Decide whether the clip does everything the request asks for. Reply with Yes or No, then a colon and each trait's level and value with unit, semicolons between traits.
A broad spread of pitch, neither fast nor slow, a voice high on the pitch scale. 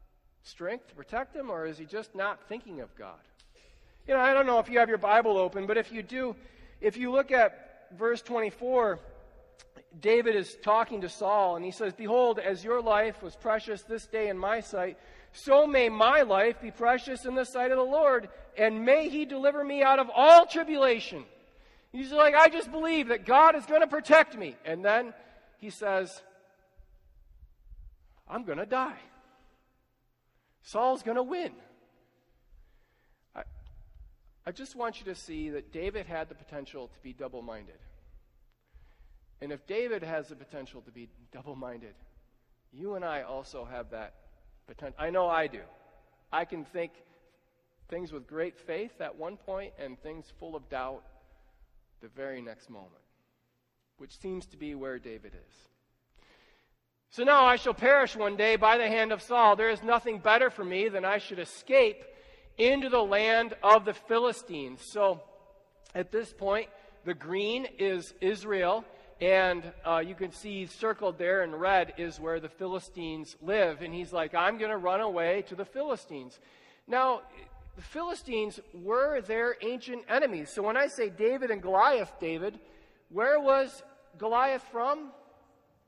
Yes: wide, 6.7 semitones; average, 170 wpm; high, 210 Hz